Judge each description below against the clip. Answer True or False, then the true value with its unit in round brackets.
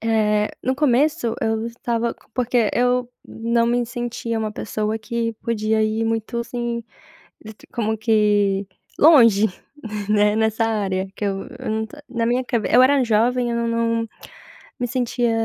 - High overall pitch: True (230 Hz)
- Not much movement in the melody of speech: True (1.8 semitones)